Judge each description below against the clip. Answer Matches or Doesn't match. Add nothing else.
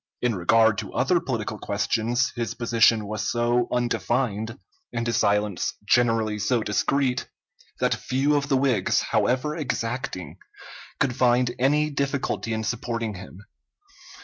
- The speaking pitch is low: Matches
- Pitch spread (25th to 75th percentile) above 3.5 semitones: Doesn't match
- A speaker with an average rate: Doesn't match